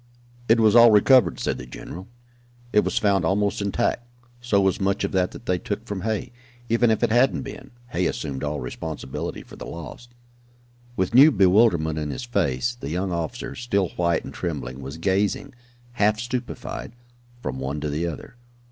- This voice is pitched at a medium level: No, low, 100 Hz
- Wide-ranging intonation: Yes, wide, 6.1 semitones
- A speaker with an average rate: Yes, average, 180 wpm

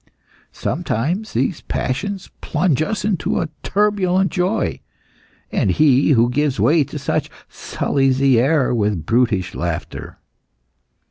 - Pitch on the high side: No, medium, 145 Hz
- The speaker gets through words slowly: Yes, slow, 120 wpm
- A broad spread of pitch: Yes, wide, 7.1 semitones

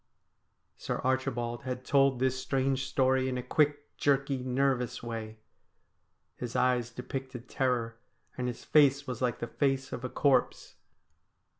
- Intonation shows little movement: Yes, narrow, 1.6 semitones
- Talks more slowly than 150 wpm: Yes, average, 140 wpm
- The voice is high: No, low, 130 Hz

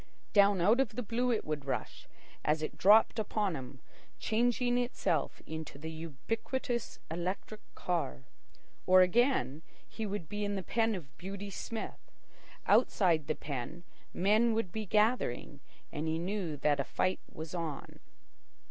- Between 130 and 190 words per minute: Yes, average, 150 wpm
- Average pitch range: No, wide, 5.7 semitones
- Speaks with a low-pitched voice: No, high, 190 Hz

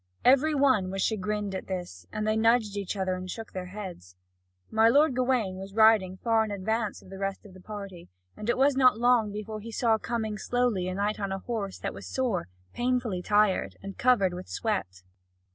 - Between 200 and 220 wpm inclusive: Yes, fast, 205 wpm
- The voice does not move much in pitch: No, average, 3.5 semitones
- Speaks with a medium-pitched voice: No, high, 210 Hz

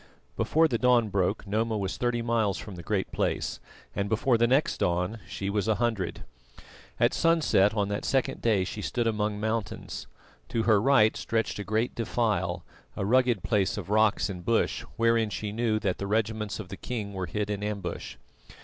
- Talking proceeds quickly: No, average, 185 wpm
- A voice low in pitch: Yes, low, 110 Hz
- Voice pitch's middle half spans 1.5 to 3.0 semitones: Yes, narrow, 2.6 semitones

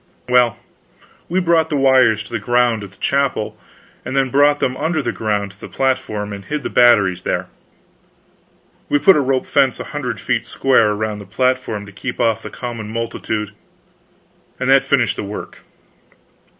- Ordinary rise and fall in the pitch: Yes, average, 4.2 semitones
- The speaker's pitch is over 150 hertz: No, low, 120 Hz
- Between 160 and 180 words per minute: Yes, average, 175 wpm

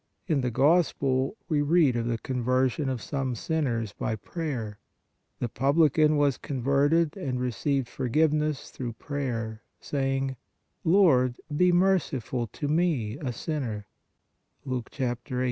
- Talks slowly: Yes, slow, 130 wpm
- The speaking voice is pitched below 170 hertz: Yes, low, 135 Hz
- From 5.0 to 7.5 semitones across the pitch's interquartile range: No, average, 3.8 semitones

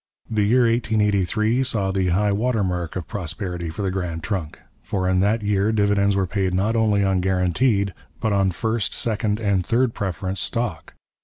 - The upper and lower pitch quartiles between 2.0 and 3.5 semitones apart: Yes, average, 2.8 semitones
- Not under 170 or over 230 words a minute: Yes, average, 175 wpm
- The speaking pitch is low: Yes, low, 100 Hz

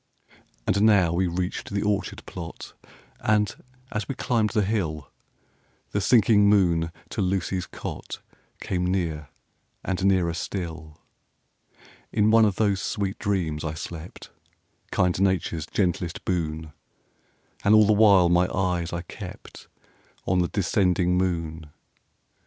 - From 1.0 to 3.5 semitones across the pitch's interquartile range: Yes, average, 3.1 semitones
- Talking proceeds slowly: Yes, slow, 130 wpm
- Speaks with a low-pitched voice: Yes, very low, 90 Hz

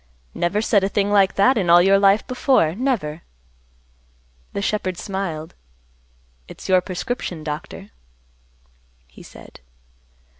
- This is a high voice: Yes, high, 195 Hz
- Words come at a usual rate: No, slow, 120 wpm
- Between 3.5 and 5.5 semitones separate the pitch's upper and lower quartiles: No, average, 3.1 semitones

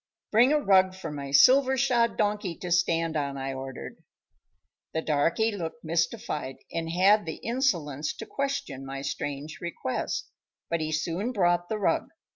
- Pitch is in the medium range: Yes, medium, 170 Hz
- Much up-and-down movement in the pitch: Yes, wide, 6.0 semitones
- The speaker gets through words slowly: No, average, 155 wpm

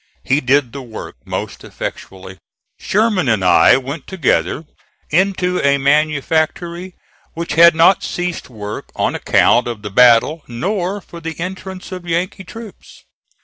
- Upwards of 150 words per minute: No, average, 140 wpm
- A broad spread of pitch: Yes, wide, 6.2 semitones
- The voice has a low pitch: No, medium, 160 Hz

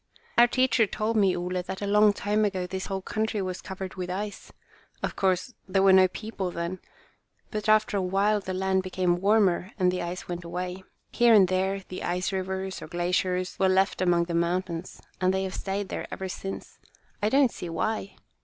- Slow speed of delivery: No, average, 200 wpm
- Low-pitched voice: No, high, 190 Hz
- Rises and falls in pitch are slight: Yes, narrow, 1.9 semitones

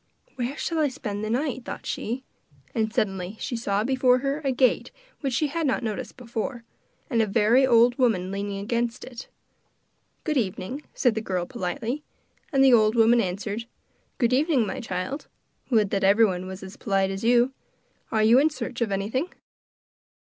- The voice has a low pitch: No, high, 230 Hz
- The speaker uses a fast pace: No, average, 175 wpm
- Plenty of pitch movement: No, average, 4.3 semitones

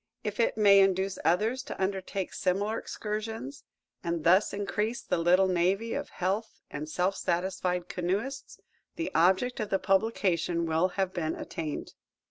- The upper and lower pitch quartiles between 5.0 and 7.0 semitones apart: No, average, 3.1 semitones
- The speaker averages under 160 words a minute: Yes, average, 145 wpm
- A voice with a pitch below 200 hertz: Yes, high, 190 Hz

